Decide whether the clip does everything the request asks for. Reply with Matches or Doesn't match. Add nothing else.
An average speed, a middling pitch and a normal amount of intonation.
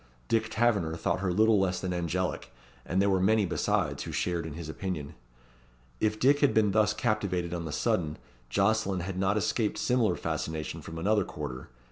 Doesn't match